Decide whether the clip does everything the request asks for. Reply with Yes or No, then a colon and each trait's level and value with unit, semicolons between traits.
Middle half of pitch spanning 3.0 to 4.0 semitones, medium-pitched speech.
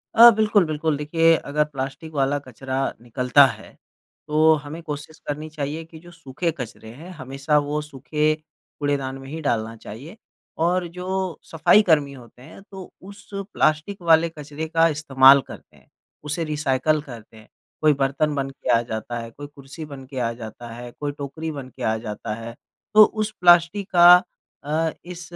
Yes: average, 3.5 semitones; medium, 150 Hz